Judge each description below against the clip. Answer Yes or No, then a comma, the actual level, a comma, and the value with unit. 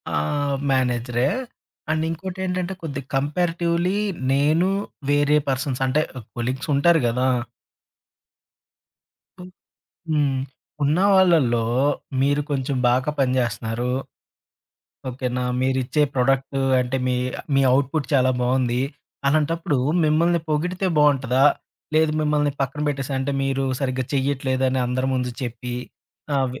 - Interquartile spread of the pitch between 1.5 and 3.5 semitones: Yes, average, 3.1 semitones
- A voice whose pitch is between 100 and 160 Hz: Yes, low, 135 Hz